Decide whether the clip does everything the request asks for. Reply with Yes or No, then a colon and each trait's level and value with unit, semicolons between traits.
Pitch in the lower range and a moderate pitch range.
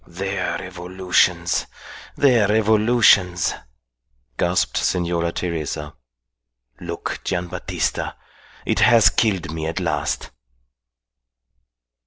Yes: very low, 90 Hz; average, 3.2 semitones